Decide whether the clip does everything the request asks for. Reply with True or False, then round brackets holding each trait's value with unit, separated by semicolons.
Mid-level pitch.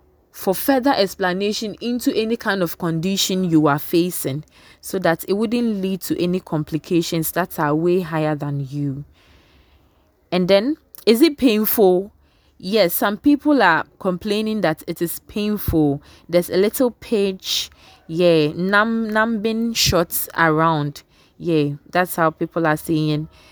True (175 Hz)